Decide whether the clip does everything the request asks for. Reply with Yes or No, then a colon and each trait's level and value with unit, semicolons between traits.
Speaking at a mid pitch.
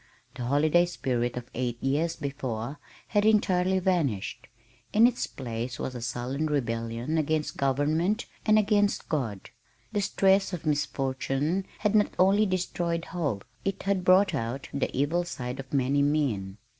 Yes: medium, 150 Hz